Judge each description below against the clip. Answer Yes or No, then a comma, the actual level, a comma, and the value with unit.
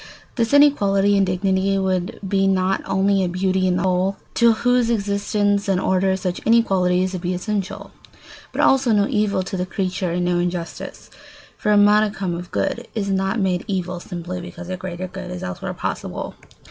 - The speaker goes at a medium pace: Yes, average, 180 wpm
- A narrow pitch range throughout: Yes, narrow, 1.9 semitones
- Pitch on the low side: No, high, 190 Hz